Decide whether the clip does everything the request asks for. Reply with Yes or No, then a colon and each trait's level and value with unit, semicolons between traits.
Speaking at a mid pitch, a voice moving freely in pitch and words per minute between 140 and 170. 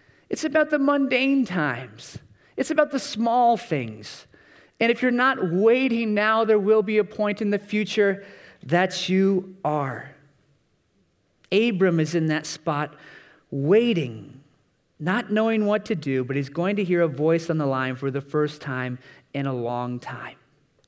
Yes: medium, 180 Hz; wide, 7.4 semitones; average, 160 wpm